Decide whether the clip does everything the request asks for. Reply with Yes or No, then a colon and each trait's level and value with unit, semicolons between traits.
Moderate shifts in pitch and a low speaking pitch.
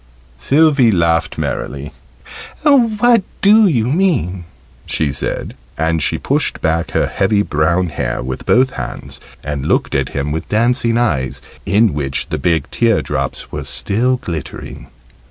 No: wide, 8.5 semitones; low, 100 Hz